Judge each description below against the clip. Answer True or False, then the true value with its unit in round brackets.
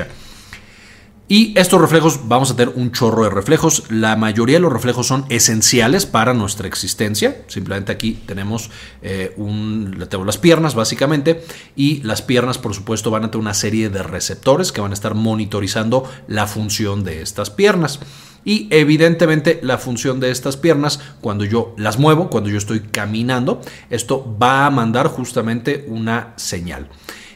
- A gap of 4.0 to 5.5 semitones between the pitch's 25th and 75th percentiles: True (4.5 semitones)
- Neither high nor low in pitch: False (115 Hz)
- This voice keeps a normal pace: True (160 wpm)